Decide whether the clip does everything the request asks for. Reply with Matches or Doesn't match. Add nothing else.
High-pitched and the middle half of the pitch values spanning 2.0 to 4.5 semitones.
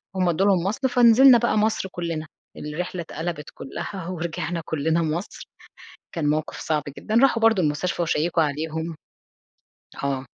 Doesn't match